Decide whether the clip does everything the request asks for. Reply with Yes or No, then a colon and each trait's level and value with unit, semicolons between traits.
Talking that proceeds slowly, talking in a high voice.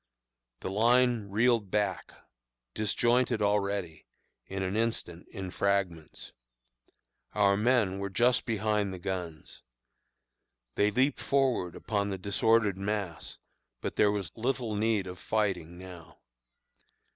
No: slow, 115 wpm; low, 100 Hz